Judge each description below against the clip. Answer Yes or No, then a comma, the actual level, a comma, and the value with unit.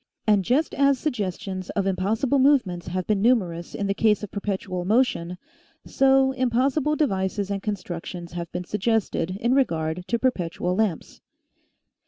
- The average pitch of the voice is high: Yes, high, 200 Hz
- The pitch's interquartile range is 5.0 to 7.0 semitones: Yes, wide, 5.6 semitones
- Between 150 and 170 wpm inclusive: Yes, average, 155 wpm